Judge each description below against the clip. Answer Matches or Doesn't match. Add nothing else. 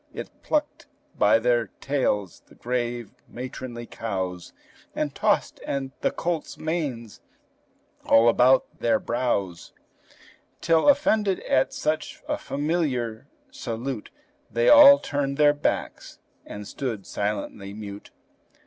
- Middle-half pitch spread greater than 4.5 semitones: Matches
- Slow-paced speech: Matches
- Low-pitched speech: Matches